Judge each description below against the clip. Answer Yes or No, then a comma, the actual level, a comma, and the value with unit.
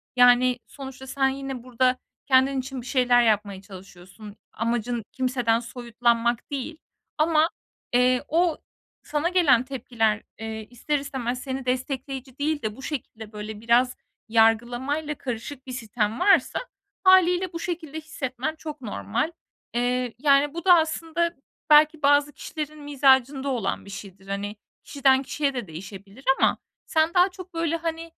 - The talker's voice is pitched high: Yes, very high, 260 Hz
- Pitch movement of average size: Yes, average, 4.4 semitones